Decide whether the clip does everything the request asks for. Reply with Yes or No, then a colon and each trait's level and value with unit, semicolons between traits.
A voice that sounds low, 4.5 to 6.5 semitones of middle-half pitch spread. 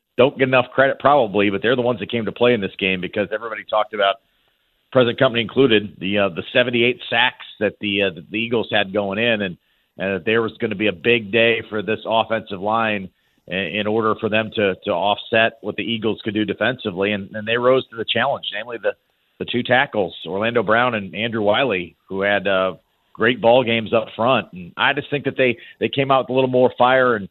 No: low, 110 Hz; average, 3.1 semitones